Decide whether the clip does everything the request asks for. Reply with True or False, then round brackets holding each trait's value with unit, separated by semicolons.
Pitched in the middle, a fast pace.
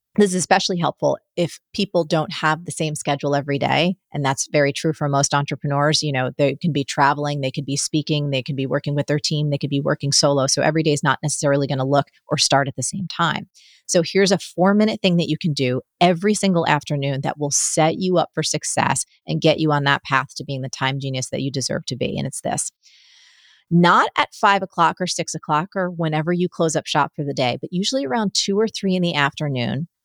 True (150 Hz; 240 wpm)